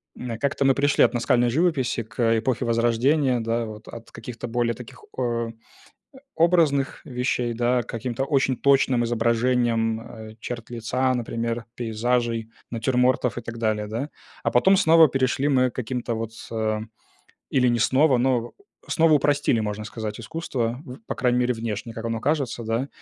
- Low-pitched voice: Yes, low, 120 Hz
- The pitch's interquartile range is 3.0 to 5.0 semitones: No, narrow, 2.4 semitones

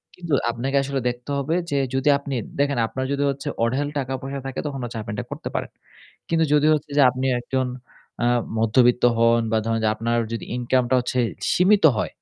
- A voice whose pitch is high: No, low, 130 Hz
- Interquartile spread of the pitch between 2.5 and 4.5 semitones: Yes, average, 2.8 semitones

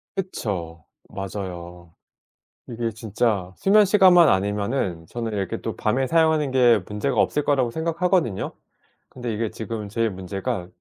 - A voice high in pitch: No, low, 115 Hz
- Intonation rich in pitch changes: Yes, wide, 6.4 semitones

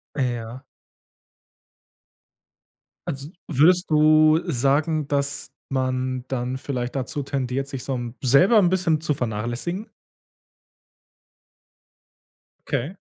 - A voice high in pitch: No, low, 135 Hz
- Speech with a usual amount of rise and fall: Yes, average, 3.4 semitones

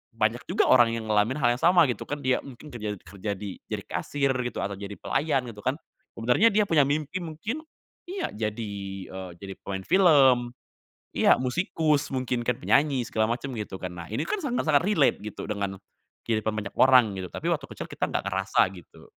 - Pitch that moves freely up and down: Yes, wide, 6.1 semitones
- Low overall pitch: Yes, low, 125 Hz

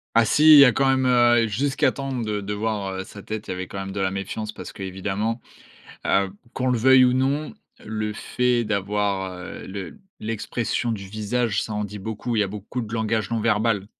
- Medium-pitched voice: No, low, 110 Hz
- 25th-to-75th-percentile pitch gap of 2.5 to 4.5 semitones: Yes, average, 3.3 semitones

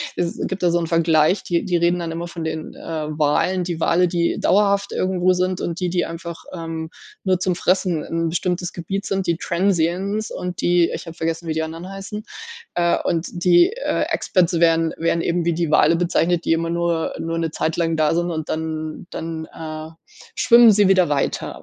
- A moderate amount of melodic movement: No, narrow, 1.8 semitones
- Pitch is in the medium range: Yes, medium, 170 Hz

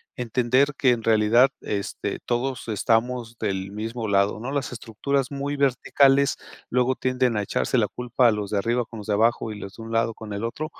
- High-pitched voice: No, low, 115 Hz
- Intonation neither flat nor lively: Yes, average, 3.1 semitones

